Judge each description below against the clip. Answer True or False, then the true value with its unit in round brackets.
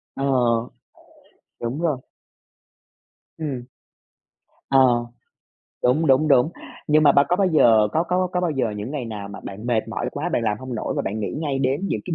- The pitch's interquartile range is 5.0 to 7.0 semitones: True (5.3 semitones)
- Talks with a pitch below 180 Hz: True (135 Hz)